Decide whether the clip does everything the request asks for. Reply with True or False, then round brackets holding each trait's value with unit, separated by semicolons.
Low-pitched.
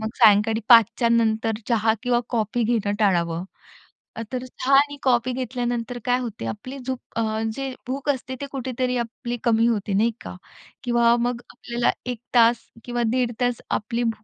False (235 Hz)